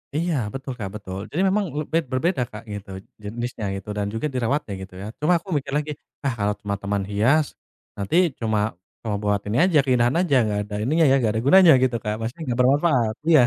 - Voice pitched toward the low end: Yes, low, 120 Hz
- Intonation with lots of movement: Yes, wide, 6.6 semitones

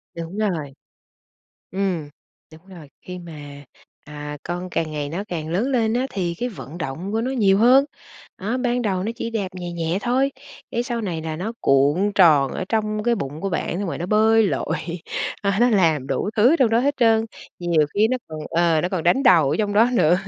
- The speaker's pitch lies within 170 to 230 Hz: Yes, medium, 185 Hz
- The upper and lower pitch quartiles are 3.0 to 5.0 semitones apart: No, wide, 5.6 semitones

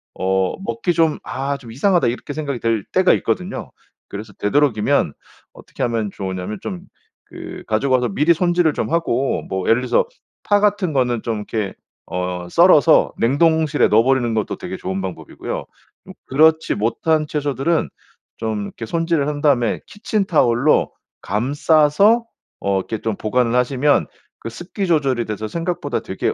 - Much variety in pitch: Yes, wide, 6.4 semitones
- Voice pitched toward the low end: Yes, low, 130 Hz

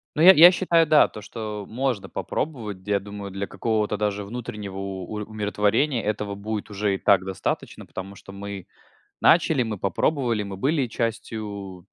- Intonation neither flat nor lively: Yes, average, 3.1 semitones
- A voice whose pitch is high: No, low, 105 Hz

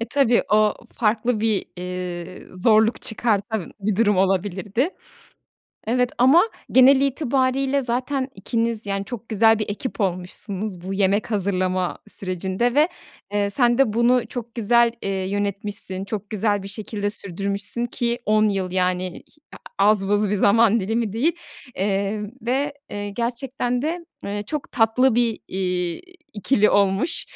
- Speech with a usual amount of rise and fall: Yes, average, 3.5 semitones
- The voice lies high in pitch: Yes, high, 215 Hz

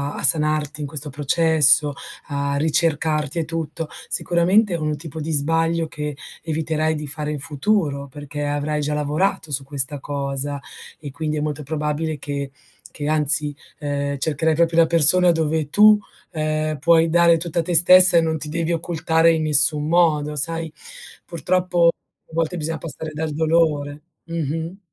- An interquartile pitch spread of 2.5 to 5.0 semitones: No, narrow, 2.0 semitones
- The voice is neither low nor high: Yes, medium, 155 Hz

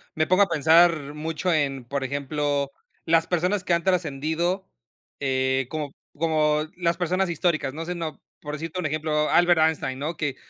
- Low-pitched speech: No, medium, 155 Hz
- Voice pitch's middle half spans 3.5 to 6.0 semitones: No, average, 3.0 semitones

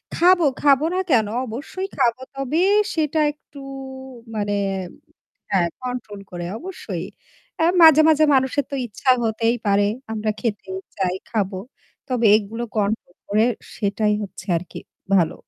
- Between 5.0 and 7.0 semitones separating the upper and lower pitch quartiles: Yes, wide, 5.6 semitones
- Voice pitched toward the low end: No, high, 225 Hz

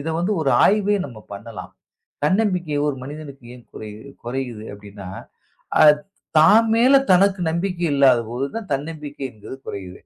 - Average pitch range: No, wide, 7.3 semitones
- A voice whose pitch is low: No, medium, 145 Hz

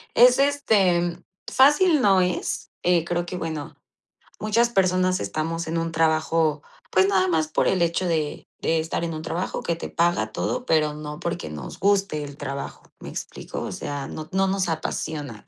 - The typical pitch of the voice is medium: Yes, medium, 170 Hz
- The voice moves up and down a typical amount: Yes, average, 3.4 semitones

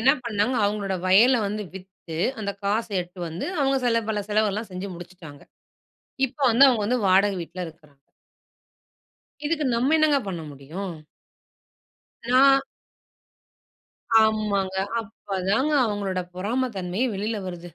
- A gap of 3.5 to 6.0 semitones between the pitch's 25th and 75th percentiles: Yes, average, 4.1 semitones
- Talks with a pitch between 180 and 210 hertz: Yes, high, 205 Hz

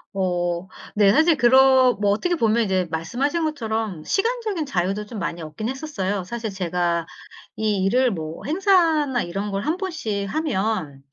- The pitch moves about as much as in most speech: No, wide, 7.6 semitones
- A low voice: No, high, 220 Hz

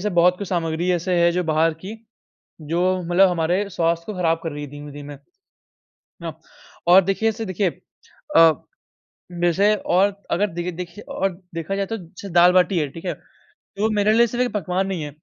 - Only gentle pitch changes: No, average, 3.1 semitones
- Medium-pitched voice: Yes, medium, 180 Hz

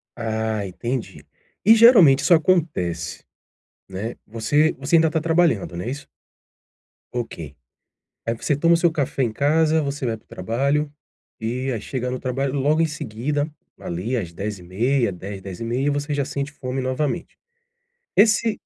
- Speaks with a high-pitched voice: No, low, 130 Hz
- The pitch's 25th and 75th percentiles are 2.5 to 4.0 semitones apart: No, average, 5.3 semitones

